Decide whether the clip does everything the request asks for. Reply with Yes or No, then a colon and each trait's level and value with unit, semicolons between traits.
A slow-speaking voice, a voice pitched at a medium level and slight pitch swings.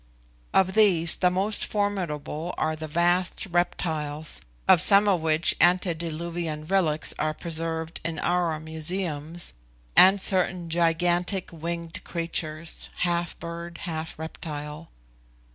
Yes: slow, 110 wpm; medium, 170 Hz; narrow, 2.1 semitones